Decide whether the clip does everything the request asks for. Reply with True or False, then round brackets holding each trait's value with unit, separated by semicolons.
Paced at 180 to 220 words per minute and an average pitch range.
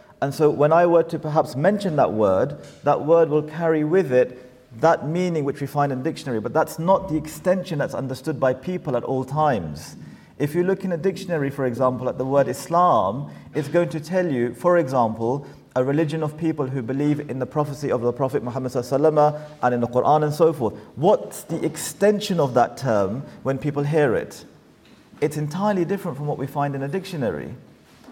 True (200 wpm; 3.7 semitones)